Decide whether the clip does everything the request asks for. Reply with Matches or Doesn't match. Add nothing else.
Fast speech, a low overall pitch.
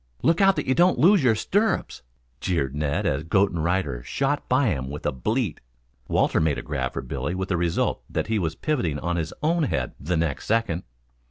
Matches